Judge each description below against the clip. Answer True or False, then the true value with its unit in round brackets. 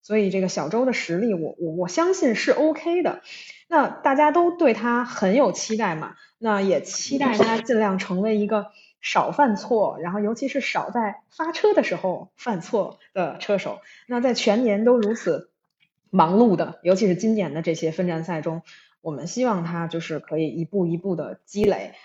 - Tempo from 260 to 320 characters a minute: True (270 characters per minute)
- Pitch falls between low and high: False (210 Hz)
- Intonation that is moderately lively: False (5.8 semitones)